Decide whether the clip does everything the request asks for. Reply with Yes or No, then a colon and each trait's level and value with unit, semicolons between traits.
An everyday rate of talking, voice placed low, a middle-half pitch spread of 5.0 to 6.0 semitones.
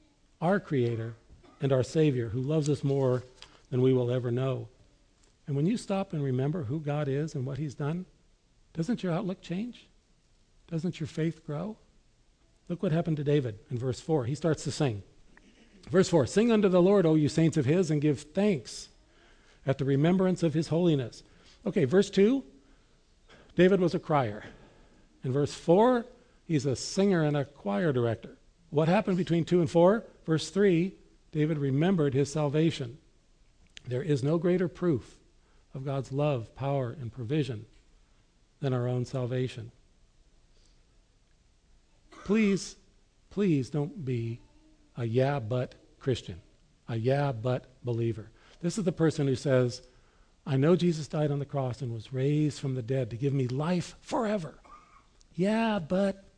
No: average, 160 wpm; medium, 150 Hz; average, 5.3 semitones